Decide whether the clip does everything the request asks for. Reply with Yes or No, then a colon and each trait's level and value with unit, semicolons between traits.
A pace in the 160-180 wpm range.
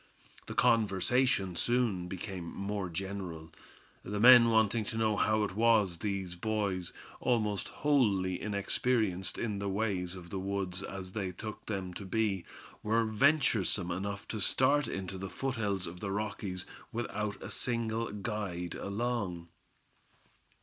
No: slow, 135 wpm